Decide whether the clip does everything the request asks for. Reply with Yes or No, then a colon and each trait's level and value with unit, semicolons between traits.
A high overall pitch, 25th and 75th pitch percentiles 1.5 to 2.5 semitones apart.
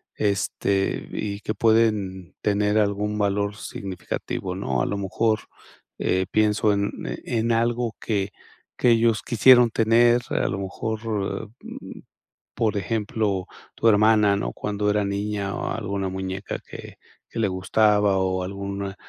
No: low, 105 Hz; narrow, 2.1 semitones